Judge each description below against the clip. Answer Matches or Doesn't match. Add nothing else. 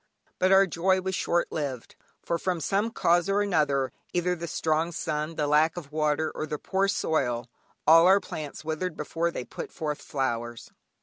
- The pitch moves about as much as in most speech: Matches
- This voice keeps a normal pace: Matches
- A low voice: Doesn't match